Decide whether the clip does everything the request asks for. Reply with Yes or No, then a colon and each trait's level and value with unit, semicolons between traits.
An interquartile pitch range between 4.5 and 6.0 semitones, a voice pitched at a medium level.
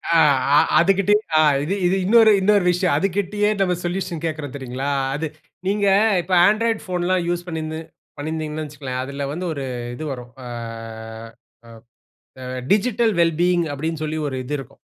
Yes: average, 4.8 semitones; medium, 170 Hz